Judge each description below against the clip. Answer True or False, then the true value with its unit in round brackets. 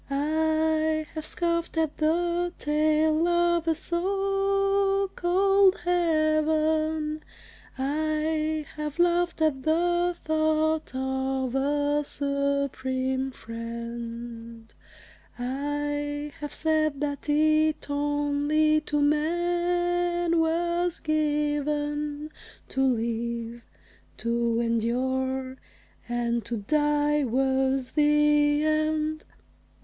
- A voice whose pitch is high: True (300 Hz)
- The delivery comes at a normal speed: False (80 wpm)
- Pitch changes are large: False (3.0 semitones)